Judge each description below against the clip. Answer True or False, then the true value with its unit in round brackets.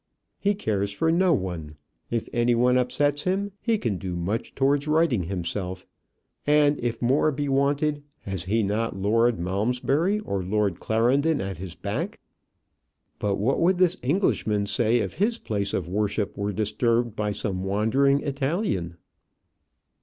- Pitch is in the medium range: False (115 Hz)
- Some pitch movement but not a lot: False (6.4 semitones)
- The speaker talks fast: False (150 wpm)